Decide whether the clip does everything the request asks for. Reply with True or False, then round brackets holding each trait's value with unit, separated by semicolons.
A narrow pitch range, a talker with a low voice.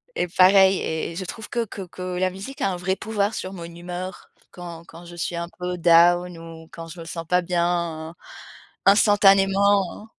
False (2.3 semitones; 180 Hz)